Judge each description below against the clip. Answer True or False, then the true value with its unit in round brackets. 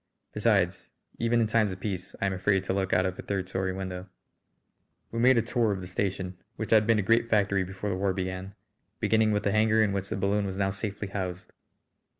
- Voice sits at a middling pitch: False (100 Hz)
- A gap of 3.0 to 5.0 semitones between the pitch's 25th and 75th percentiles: False (2.4 semitones)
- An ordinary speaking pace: False (225 wpm)